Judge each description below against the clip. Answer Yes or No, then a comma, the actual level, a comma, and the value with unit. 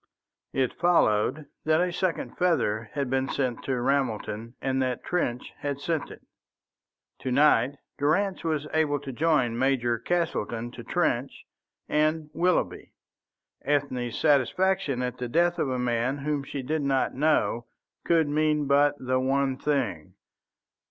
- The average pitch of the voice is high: No, medium, 140 Hz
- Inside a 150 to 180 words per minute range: No, average, 140 wpm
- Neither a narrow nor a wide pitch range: Yes, average, 3.6 semitones